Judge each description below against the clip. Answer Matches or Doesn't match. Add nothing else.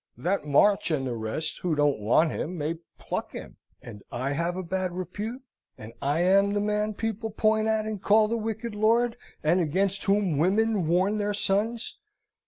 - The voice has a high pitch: Matches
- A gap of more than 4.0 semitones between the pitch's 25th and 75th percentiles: Matches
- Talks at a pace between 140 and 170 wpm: Doesn't match